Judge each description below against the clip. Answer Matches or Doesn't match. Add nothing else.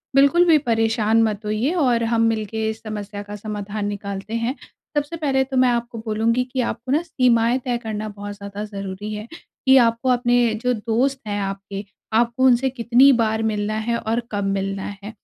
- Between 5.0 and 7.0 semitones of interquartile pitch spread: Doesn't match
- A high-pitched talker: Matches